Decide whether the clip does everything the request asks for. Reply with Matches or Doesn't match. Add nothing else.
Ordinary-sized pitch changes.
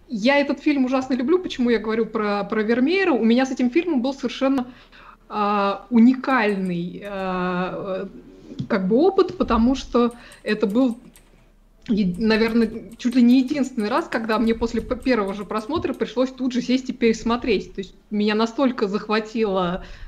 Matches